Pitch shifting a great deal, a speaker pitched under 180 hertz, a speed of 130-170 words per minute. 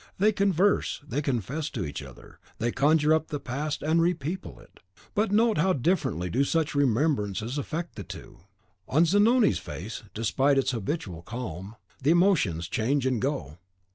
Yes: wide, 6.5 semitones; medium, 140 Hz; average, 160 wpm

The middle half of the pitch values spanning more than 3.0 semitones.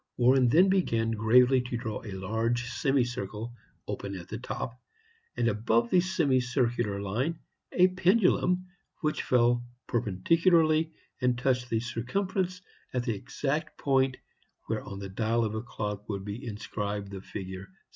Yes: average, 4.6 semitones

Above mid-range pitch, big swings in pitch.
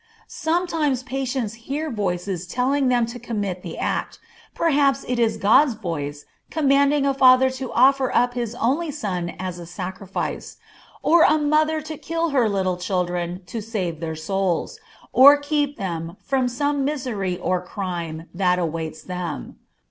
Yes: high, 235 Hz; wide, 7.4 semitones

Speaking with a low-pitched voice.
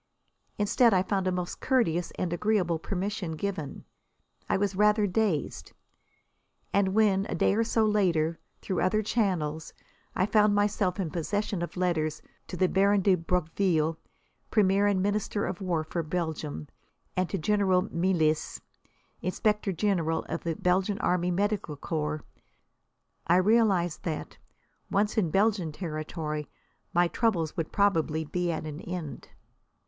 No: medium, 185 Hz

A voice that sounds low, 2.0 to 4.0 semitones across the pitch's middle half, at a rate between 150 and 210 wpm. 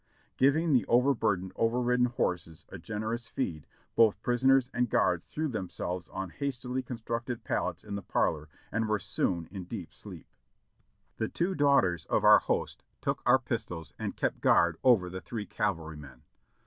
No: low, 110 Hz; wide, 5.6 semitones; average, 160 wpm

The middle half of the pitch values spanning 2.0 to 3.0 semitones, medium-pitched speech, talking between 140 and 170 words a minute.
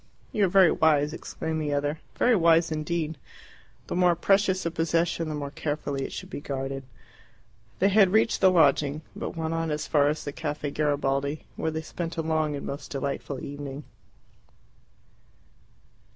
Yes: average, 2.7 semitones; medium, 155 Hz; average, 165 wpm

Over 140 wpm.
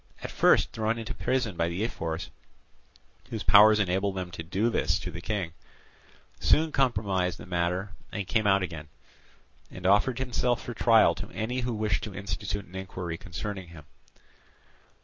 Yes: average, 165 wpm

